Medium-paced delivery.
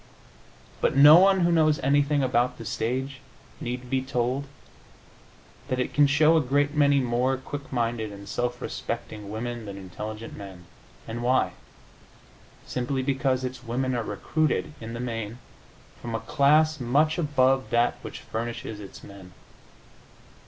Yes: average, 145 wpm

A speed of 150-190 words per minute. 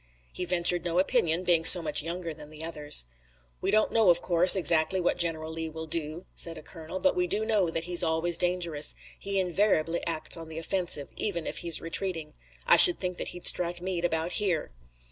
No: fast, 205 wpm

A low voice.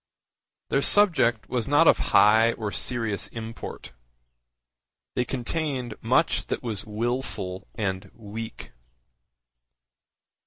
Yes: low, 115 Hz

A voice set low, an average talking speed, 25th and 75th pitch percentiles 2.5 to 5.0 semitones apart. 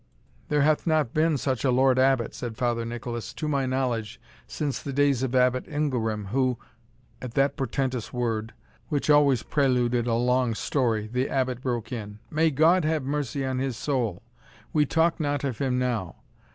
Yes: low, 130 Hz; average, 180 wpm; average, 3.1 semitones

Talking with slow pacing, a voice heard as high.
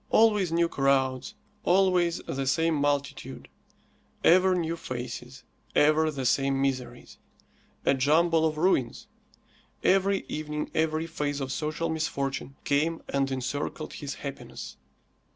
No: slow, 115 wpm; medium, 150 Hz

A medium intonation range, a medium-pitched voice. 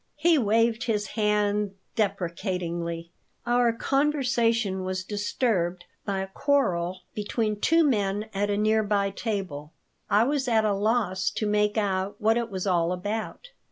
No: average, 3.3 semitones; high, 210 Hz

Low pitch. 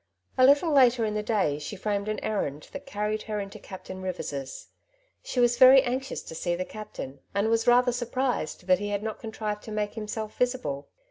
No: high, 215 Hz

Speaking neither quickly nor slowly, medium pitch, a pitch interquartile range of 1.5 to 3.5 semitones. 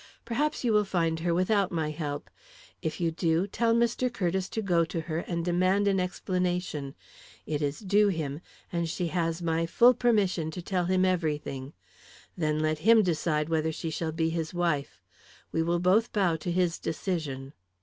Yes: average, 180 wpm; medium, 170 Hz; average, 3.0 semitones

